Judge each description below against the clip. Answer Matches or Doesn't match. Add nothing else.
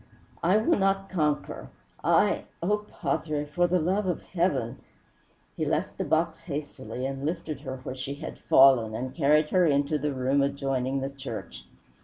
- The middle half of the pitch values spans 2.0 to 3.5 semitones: Doesn't match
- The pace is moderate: Matches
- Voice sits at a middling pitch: Matches